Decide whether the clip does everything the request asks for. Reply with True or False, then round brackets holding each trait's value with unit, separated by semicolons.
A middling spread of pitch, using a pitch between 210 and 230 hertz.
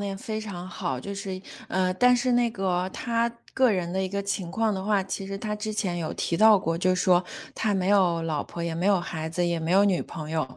False (3.2 semitones; 190 Hz)